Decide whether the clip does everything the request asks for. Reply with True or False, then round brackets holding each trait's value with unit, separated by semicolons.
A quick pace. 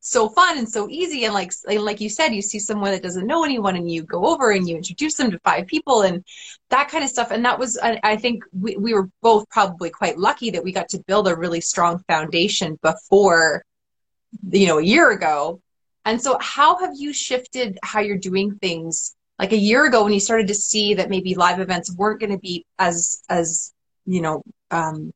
True (220 wpm)